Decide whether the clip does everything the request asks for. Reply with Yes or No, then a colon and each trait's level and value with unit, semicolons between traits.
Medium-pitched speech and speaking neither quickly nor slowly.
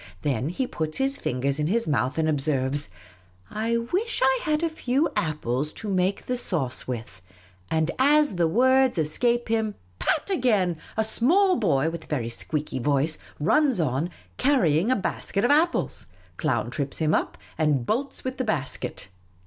Yes: medium, 170 Hz; average, 180 wpm